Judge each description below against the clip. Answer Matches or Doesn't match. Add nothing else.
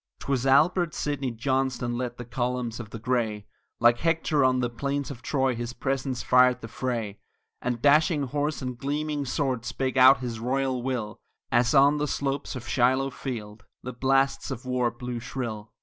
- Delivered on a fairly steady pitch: Matches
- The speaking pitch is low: Matches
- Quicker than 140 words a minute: Matches